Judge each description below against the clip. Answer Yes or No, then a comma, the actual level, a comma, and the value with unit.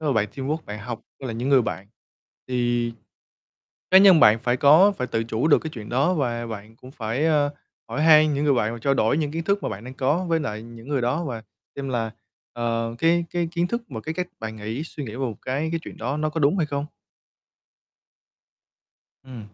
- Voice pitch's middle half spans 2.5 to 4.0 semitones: No, average, 5.1 semitones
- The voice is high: No, low, 135 Hz